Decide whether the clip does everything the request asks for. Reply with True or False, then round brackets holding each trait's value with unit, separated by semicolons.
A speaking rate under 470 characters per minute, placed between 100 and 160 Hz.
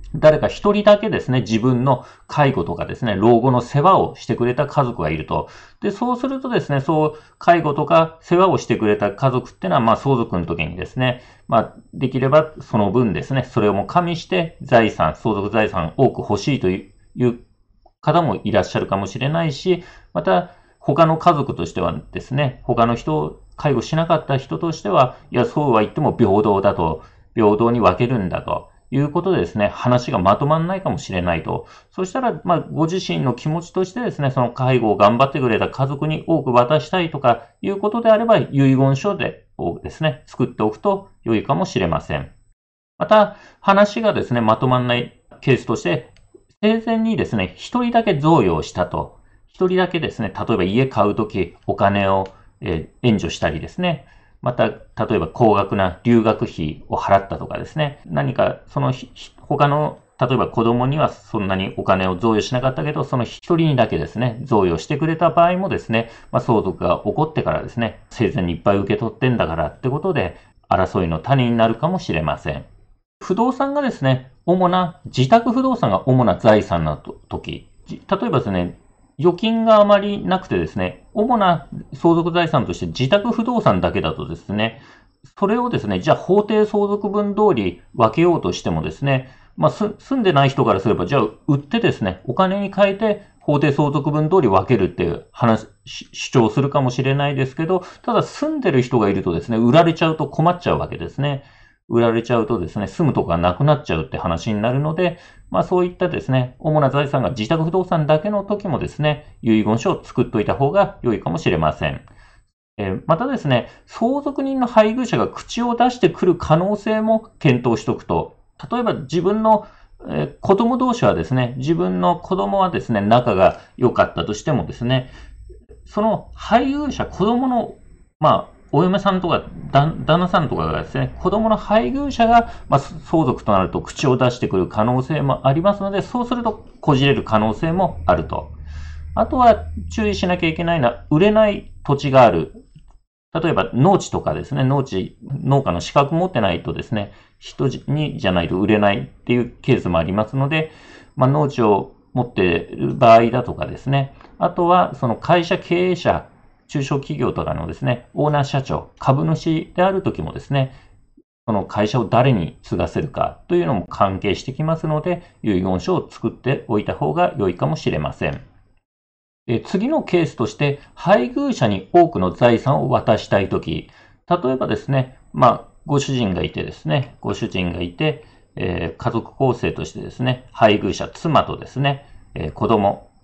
True (360 characters per minute; 140 Hz)